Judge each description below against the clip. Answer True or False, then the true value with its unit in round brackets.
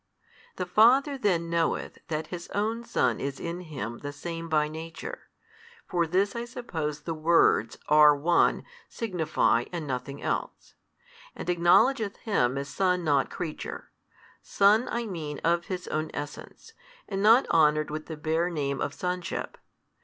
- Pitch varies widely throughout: False (4.2 semitones)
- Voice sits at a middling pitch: True (170 Hz)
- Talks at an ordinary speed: True (150 wpm)